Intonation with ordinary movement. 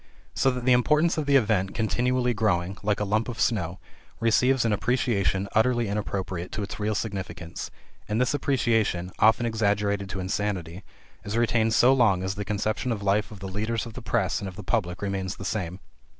Yes: average, 3.3 semitones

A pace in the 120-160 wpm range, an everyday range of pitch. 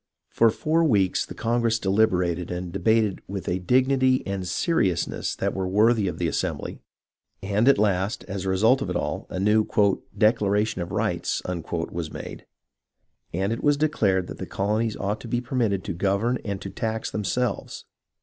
No: average, 175 wpm; average, 3.6 semitones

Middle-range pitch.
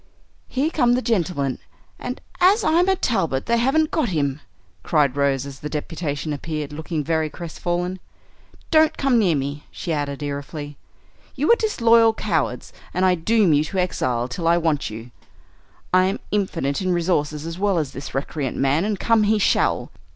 Yes: medium, 170 Hz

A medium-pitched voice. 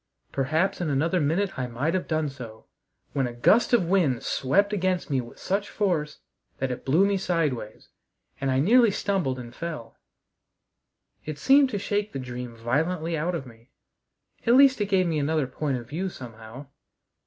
Yes: medium, 155 Hz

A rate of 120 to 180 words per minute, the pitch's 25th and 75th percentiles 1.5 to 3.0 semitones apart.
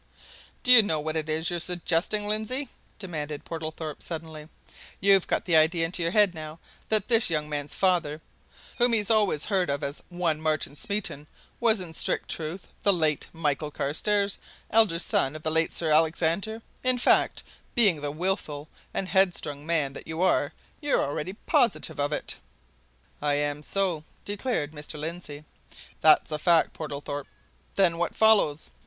No: average, 165 wpm; average, 4.4 semitones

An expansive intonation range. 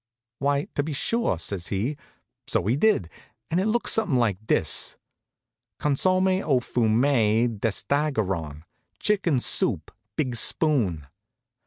Yes: wide, 6.6 semitones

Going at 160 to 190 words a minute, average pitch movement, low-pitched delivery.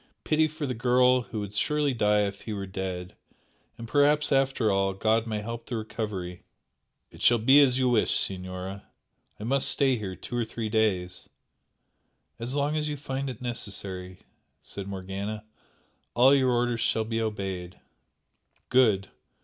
Yes: average, 165 wpm; average, 4.7 semitones; low, 110 Hz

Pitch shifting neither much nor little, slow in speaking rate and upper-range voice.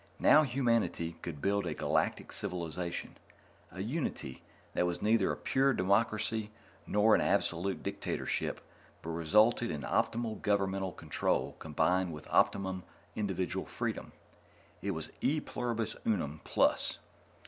No: average, 4.6 semitones; slow, 125 wpm; low, 100 Hz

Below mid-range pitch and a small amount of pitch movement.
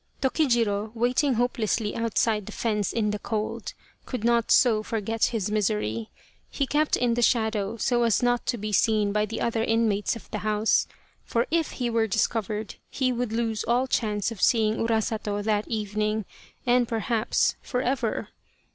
No: high, 225 Hz; narrow, 2.1 semitones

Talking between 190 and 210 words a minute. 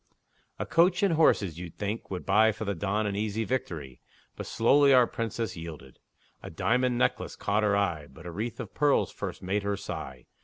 Yes: average, 195 wpm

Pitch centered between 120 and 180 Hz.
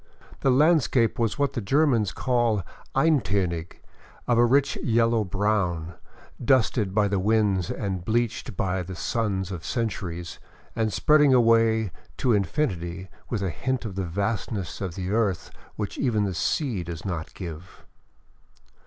No: low, 105 Hz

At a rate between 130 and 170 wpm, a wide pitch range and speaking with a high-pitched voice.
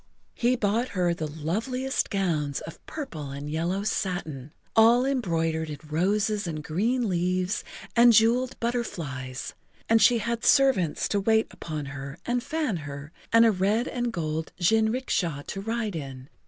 Yes: average, 150 wpm; wide, 6.8 semitones; high, 195 Hz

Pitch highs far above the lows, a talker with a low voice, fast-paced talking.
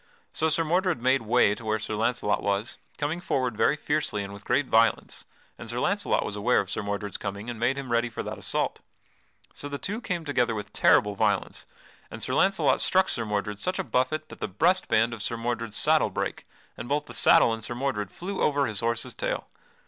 Yes: wide, 5.7 semitones; low, 120 Hz; fast, 215 wpm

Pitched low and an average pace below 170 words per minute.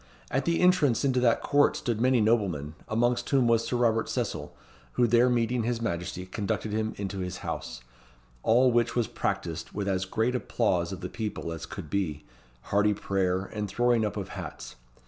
No: low, 110 Hz; average, 185 wpm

